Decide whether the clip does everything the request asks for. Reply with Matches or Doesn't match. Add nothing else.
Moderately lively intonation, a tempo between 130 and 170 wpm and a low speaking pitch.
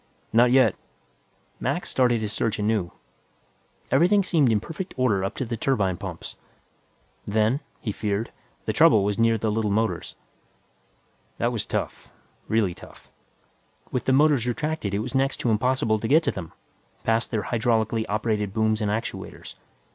Matches